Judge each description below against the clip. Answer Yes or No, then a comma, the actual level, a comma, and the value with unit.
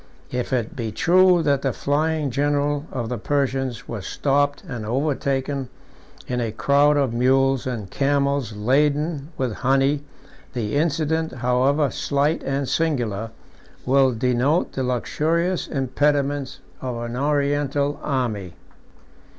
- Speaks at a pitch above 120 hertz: Yes, low, 135 Hz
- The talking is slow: Yes, slow, 125 wpm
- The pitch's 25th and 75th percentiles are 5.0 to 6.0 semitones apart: No, narrow, 2.6 semitones